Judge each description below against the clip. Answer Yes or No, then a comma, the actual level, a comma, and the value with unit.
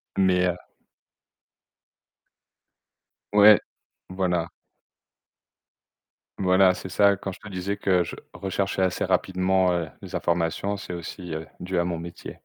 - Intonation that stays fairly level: Yes, narrow, 1.7 semitones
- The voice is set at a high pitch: No, very low, 90 Hz